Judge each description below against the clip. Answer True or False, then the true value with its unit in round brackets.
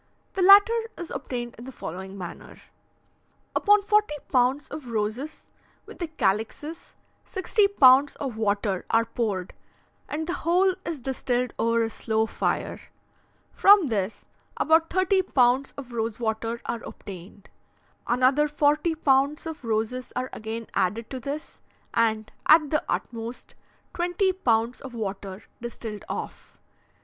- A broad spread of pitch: True (5.9 semitones)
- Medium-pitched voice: False (250 Hz)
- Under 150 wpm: True (135 wpm)